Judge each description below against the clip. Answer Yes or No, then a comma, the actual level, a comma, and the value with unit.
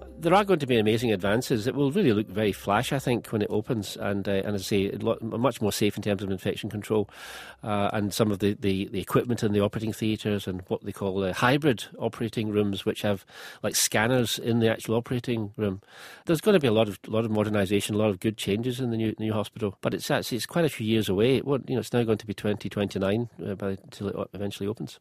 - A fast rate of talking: Yes, fast, 250 wpm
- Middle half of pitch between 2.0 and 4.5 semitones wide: Yes, narrow, 2.5 semitones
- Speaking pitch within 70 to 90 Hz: No, low, 110 Hz